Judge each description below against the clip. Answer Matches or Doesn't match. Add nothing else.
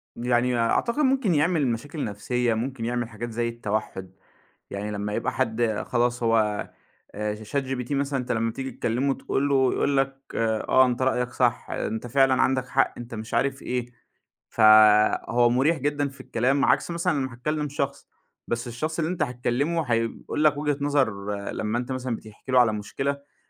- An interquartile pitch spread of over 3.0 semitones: Matches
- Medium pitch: Doesn't match